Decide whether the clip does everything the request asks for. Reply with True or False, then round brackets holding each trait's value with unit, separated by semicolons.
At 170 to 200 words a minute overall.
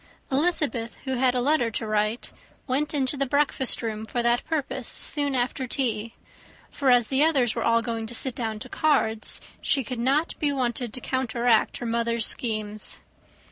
True (180 wpm)